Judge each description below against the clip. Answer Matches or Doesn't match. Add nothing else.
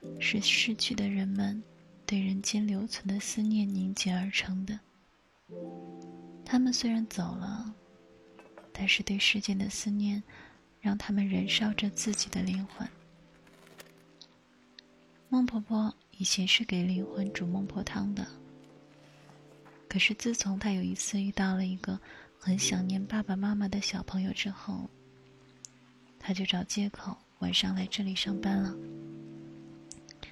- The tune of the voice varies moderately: Doesn't match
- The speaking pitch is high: Matches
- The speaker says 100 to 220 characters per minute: Matches